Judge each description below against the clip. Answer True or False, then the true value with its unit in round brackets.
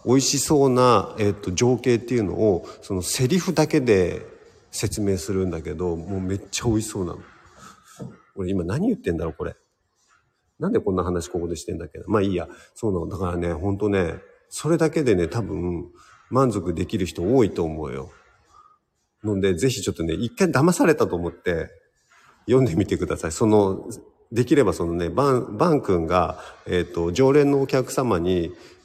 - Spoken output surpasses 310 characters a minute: True (345 characters per minute)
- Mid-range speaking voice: False (100 Hz)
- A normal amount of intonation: False (6.3 semitones)